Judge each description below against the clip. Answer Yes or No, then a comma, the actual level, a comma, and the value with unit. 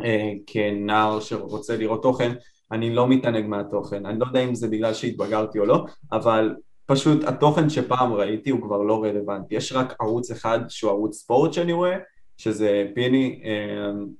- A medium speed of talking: No, fast, 165 wpm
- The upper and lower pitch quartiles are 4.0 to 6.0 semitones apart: No, average, 3.1 semitones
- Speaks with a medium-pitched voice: No, low, 115 Hz